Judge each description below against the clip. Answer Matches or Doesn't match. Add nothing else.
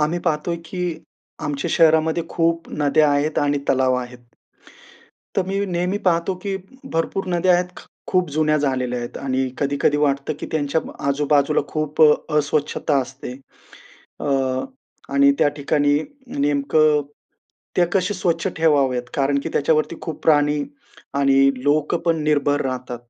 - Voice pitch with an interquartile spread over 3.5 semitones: Doesn't match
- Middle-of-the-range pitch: Matches